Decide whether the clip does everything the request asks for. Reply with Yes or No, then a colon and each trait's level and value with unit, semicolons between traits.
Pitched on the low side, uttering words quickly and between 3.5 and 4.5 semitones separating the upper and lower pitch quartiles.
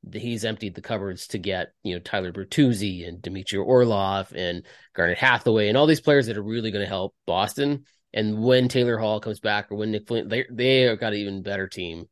Yes: low, 110 Hz; fast, 225 wpm; average, 3.8 semitones